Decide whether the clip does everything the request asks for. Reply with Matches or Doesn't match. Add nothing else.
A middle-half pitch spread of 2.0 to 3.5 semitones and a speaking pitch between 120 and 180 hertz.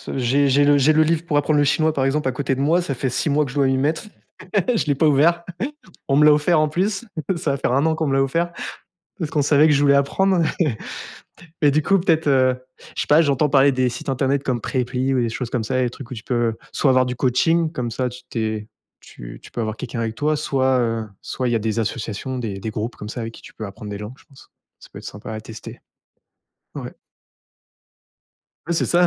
Doesn't match